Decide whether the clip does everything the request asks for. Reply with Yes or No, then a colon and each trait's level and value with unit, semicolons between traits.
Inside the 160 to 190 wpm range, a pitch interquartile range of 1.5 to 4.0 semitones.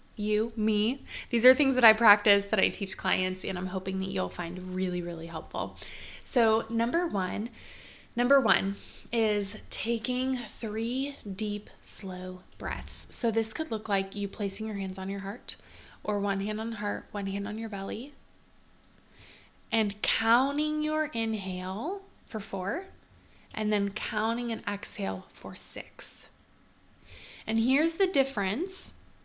No: average, 145 wpm; average, 3.4 semitones